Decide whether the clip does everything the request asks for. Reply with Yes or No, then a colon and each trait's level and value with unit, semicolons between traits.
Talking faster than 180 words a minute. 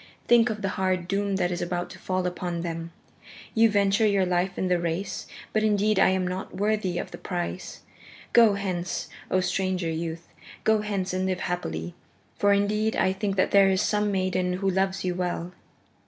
Yes: average, 190 wpm